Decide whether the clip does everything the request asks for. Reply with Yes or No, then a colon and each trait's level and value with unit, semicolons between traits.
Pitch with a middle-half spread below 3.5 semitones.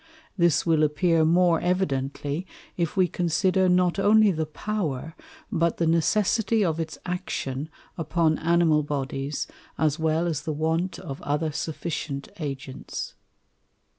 Yes: average, 3.0 semitones